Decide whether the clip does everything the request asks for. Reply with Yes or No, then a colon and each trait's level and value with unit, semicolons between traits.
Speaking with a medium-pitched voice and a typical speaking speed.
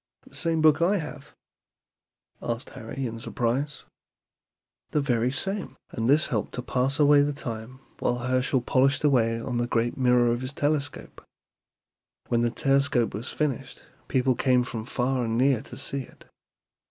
No: low, 130 Hz; average, 165 wpm